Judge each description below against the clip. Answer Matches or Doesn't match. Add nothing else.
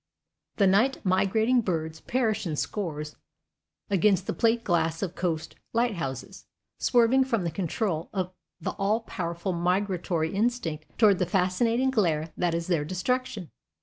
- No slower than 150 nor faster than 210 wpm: Doesn't match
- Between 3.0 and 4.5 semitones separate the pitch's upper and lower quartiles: Doesn't match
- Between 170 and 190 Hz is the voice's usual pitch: Matches